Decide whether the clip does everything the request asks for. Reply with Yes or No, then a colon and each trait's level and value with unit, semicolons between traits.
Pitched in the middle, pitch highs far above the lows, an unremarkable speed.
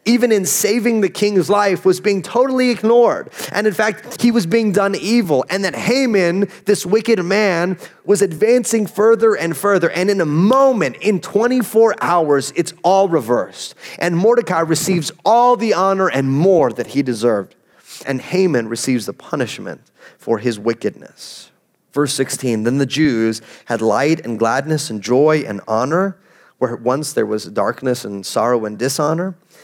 Yes: medium, 180 Hz; wide, 7.7 semitones; average, 165 wpm